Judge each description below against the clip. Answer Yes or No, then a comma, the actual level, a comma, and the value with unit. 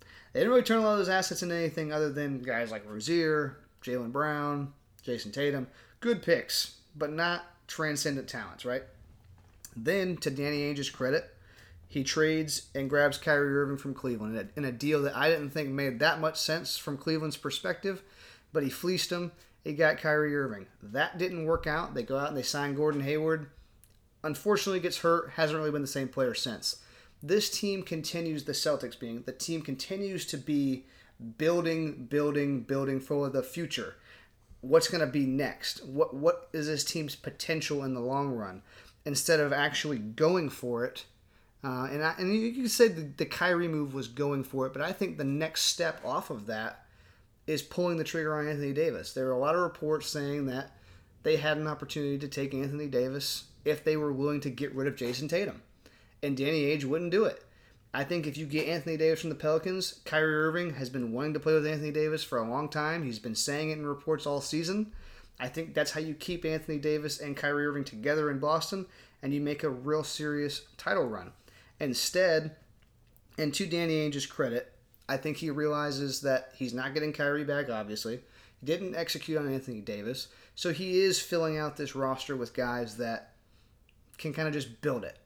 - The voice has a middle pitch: Yes, medium, 145 Hz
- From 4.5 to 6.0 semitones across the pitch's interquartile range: No, average, 3.2 semitones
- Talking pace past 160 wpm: Yes, average, 195 wpm